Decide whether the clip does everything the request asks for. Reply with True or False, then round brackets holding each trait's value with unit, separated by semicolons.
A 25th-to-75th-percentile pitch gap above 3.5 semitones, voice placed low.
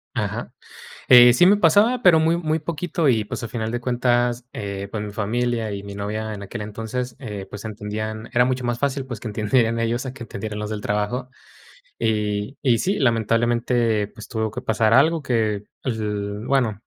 False (3.2 semitones; 115 Hz)